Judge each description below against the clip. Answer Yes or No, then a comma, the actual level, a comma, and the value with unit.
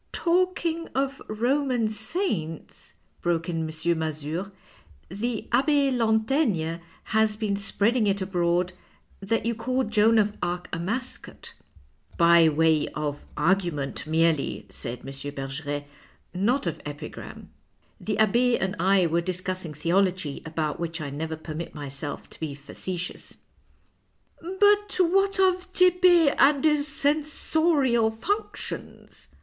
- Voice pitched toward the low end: No, high, 195 Hz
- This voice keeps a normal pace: No, slow, 130 wpm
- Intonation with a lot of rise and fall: Yes, wide, 8.4 semitones